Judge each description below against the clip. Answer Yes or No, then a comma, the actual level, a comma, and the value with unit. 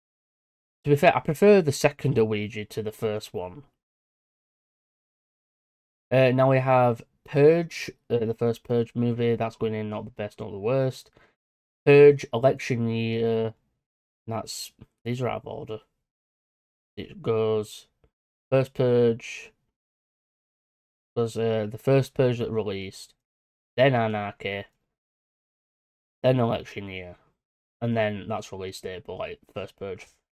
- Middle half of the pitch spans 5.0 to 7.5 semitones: No, average, 3.3 semitones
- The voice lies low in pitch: Yes, low, 115 Hz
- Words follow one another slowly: Yes, slow, 130 wpm